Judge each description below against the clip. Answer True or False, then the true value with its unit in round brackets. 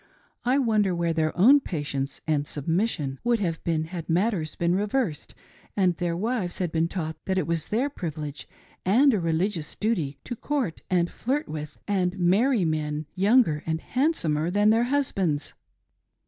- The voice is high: False (180 Hz)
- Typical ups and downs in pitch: False (5.7 semitones)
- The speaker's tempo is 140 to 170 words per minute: True (160 wpm)